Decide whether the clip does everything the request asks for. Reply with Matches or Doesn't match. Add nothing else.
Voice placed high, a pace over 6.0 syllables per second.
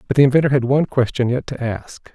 Doesn't match